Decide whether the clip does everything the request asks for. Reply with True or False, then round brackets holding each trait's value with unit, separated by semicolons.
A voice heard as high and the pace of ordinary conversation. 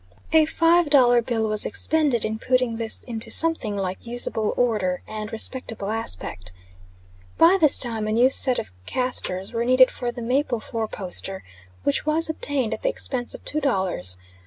True (235 Hz; 170 wpm)